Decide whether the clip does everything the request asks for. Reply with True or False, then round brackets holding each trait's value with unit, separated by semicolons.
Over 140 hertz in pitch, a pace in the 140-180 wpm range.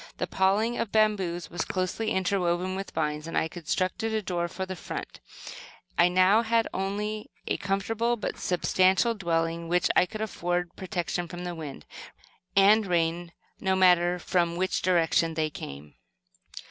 True (185 Hz; 160 wpm)